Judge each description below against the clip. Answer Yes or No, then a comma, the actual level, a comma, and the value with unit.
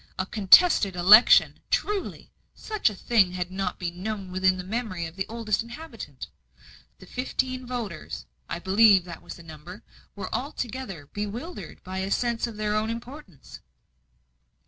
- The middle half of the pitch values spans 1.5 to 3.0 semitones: No, average, 4.3 semitones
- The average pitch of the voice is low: No, high, 205 Hz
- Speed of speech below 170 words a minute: Yes, average, 150 wpm